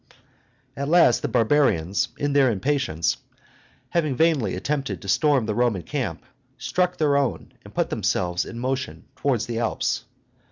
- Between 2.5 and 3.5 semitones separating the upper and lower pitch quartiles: No, average, 4.6 semitones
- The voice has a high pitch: No, low, 130 Hz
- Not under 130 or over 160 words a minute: Yes, average, 150 wpm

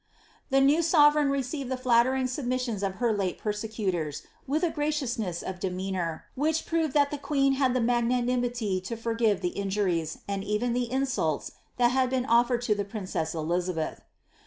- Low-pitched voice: No, high, 240 Hz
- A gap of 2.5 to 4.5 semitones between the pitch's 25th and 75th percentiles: No, average, 5.3 semitones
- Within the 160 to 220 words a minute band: Yes, average, 165 wpm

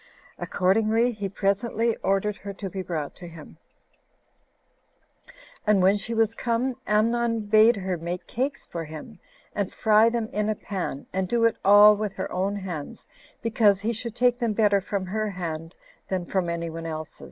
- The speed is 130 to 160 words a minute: No, average, 175 wpm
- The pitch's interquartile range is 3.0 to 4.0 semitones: Yes, average, 3.4 semitones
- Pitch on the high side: Yes, high, 205 Hz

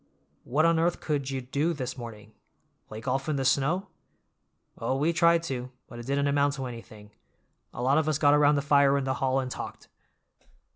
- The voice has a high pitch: No, medium, 140 Hz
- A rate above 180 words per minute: Yes, average, 200 wpm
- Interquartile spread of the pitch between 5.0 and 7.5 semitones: No, average, 2.7 semitones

